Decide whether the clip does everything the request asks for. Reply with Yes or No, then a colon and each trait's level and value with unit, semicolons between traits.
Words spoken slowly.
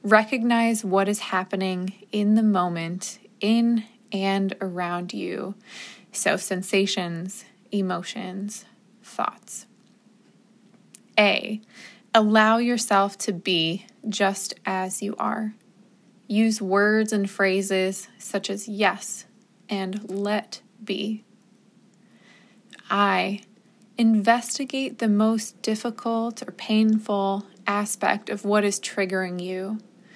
Yes: slow, 95 wpm